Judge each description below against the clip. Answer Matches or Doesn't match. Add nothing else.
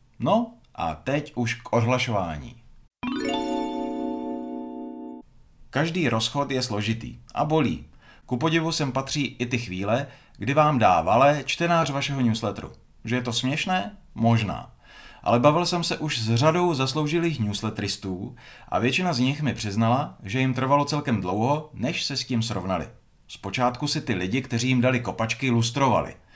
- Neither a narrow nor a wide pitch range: Matches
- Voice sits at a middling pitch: Doesn't match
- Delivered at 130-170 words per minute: Matches